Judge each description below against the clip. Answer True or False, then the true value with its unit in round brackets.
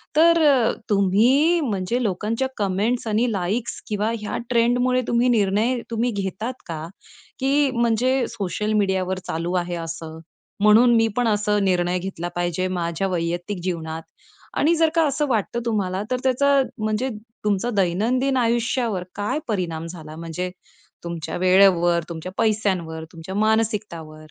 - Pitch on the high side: True (205 Hz)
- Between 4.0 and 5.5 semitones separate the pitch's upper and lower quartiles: True (5.1 semitones)